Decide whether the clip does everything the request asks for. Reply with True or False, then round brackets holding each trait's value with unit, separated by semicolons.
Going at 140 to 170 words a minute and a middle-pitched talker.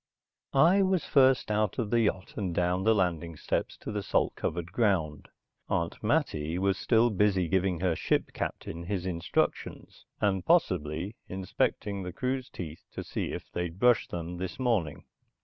False (165 wpm; 95 Hz)